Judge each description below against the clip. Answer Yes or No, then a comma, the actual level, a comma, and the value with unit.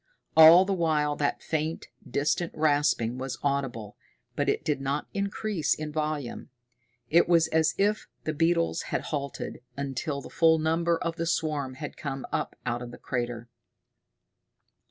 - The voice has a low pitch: No, medium, 150 Hz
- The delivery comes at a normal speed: Yes, average, 155 wpm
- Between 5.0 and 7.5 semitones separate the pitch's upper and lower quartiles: No, average, 3.2 semitones